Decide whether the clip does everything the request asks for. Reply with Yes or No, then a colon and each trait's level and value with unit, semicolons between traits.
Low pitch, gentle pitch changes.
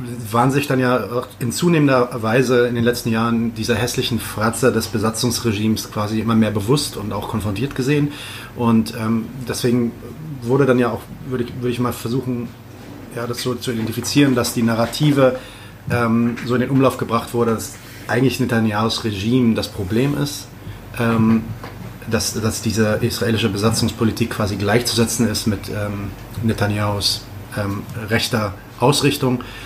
Yes: low, 115 Hz; narrow, 2.0 semitones